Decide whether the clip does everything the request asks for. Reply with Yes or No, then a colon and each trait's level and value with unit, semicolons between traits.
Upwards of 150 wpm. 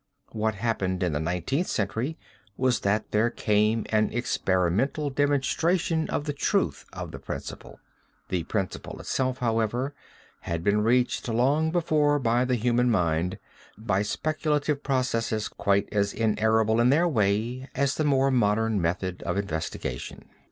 No: average, 140 wpm